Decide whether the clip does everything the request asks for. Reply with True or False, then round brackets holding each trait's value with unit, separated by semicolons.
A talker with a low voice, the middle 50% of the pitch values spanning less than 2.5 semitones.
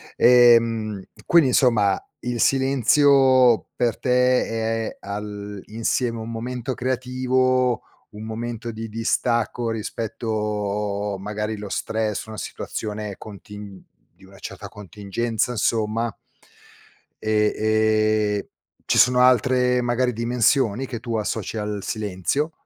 False (115 Hz; 2.8 semitones)